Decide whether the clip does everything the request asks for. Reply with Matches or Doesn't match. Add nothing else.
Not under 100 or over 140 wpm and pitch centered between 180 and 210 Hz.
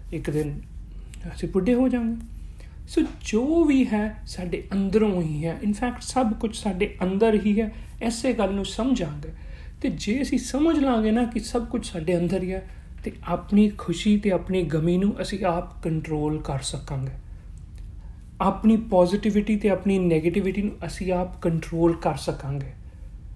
Doesn't match